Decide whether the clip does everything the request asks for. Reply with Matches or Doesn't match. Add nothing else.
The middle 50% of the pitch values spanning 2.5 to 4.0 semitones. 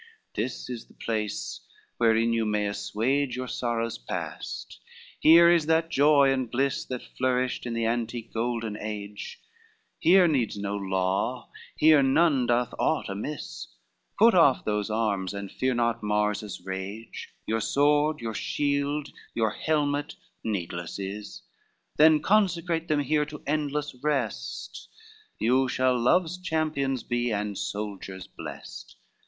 Doesn't match